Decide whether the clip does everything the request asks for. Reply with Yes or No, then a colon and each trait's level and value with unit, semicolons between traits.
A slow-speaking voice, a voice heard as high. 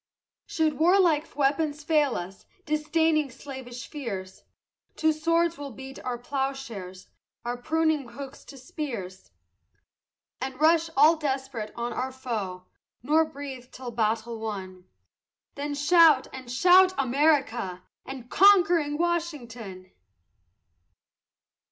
Yes: slow, 110 wpm; very high, 275 Hz